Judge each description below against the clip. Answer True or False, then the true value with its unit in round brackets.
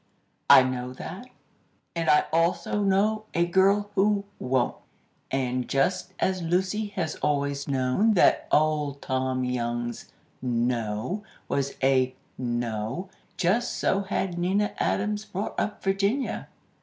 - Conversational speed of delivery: False (120 wpm)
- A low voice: False (165 Hz)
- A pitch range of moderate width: False (7.2 semitones)